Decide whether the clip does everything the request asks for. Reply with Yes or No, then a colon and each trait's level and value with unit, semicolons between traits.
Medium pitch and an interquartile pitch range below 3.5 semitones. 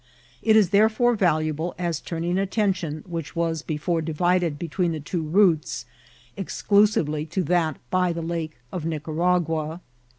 Yes: medium, 170 Hz; average, 2.7 semitones